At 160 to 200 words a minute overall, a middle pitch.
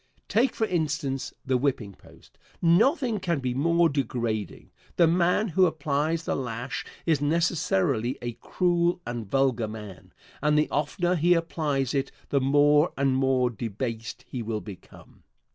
No: average, 145 wpm; medium, 145 Hz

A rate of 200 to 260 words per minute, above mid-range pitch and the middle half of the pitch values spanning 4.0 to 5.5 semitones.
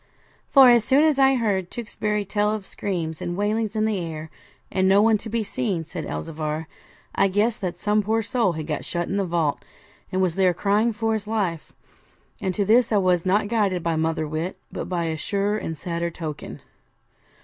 Yes: fast, 205 wpm; high, 195 Hz; average, 4.3 semitones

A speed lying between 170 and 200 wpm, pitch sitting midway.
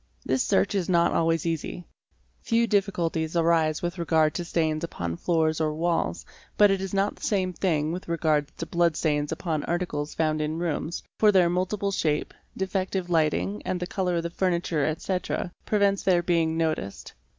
Yes: average, 180 wpm; medium, 170 Hz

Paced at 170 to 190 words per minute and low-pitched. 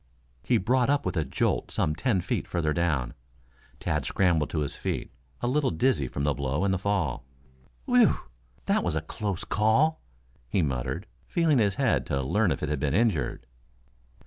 Yes: average, 180 wpm; very low, 90 Hz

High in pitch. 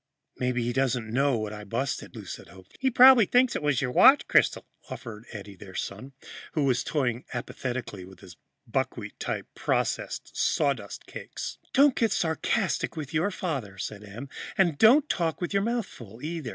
No: low, 130 Hz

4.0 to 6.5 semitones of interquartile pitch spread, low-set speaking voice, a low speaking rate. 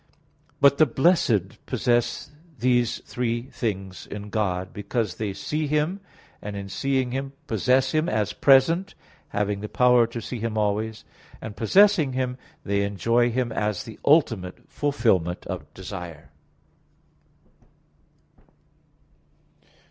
Yes: average, 4.5 semitones; low, 115 Hz; slow, 120 wpm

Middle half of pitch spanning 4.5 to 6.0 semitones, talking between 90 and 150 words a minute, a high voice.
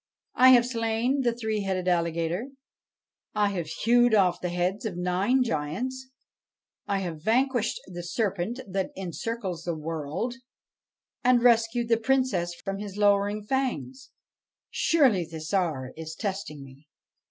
Yes: wide, 5.5 semitones; slow, 135 wpm; high, 200 Hz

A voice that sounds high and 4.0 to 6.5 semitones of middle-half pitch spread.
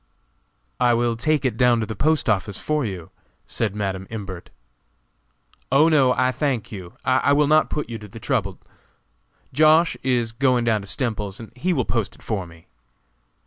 No: low, 120 Hz; average, 4.7 semitones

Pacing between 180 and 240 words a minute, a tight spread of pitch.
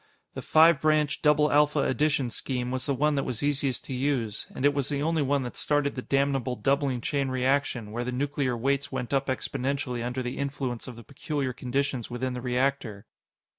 Yes: average, 200 wpm; narrow, 2.3 semitones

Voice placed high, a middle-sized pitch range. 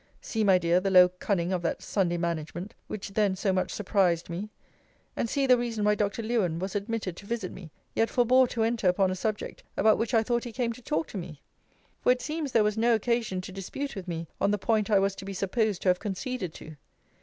Yes: high, 205 Hz; average, 3.9 semitones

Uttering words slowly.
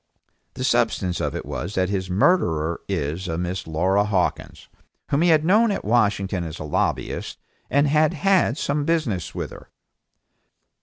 No: average, 155 wpm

